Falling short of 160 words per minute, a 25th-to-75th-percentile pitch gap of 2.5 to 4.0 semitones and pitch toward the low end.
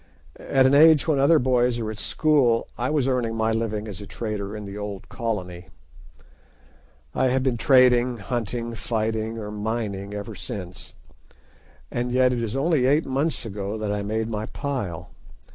No: average, 170 wpm; average, 3.5 semitones; low, 115 Hz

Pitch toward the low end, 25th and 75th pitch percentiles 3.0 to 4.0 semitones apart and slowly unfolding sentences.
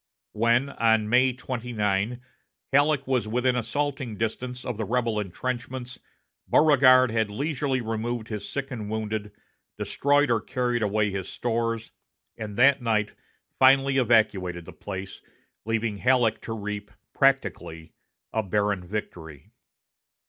Yes: low, 115 Hz; average, 3.3 semitones; slow, 125 wpm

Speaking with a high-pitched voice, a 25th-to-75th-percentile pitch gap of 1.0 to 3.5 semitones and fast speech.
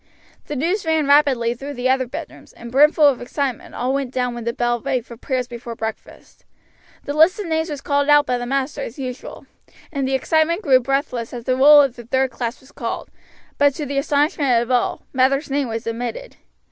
Yes: very high, 265 Hz; average, 2.9 semitones; fast, 210 wpm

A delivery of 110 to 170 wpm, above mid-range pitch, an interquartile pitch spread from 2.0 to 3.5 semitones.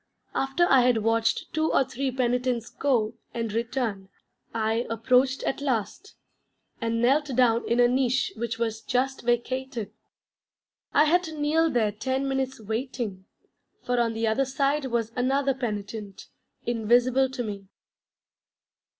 Yes: average, 140 wpm; high, 245 Hz; average, 2.9 semitones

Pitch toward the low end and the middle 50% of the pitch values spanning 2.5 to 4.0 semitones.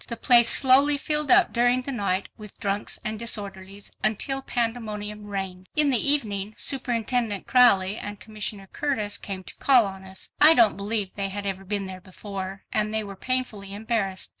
No: high, 210 Hz; average, 3.7 semitones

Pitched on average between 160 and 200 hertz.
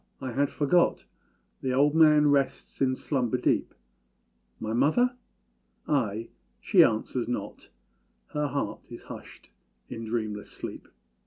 No: low, 135 Hz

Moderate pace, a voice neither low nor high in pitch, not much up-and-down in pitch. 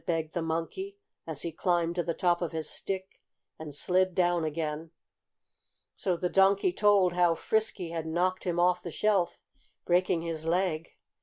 Yes: average, 165 wpm; medium, 175 Hz; narrow, 2.1 semitones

